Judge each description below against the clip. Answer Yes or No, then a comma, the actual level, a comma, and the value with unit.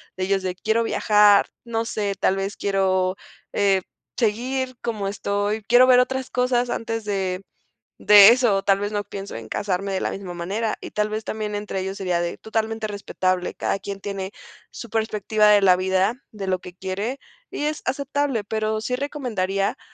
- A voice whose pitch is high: Yes, high, 205 Hz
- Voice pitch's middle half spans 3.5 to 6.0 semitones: No, average, 2.7 semitones